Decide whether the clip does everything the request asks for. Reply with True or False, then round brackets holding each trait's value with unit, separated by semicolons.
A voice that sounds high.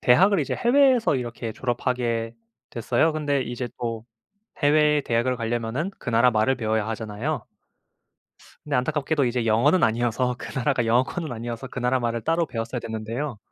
False (125 Hz)